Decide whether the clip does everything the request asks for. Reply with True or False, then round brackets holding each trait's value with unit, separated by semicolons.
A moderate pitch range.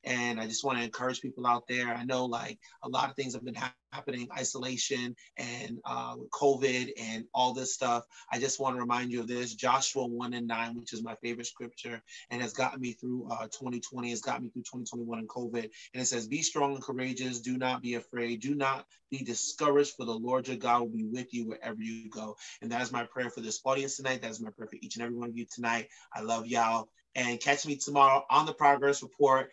False (1.9 semitones)